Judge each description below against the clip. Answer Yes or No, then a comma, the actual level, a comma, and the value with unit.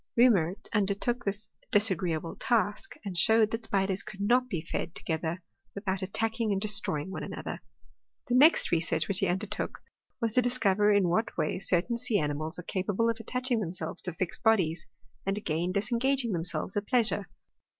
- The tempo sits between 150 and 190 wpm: Yes, average, 170 wpm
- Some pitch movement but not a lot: Yes, average, 4.3 semitones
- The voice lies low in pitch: No, high, 200 Hz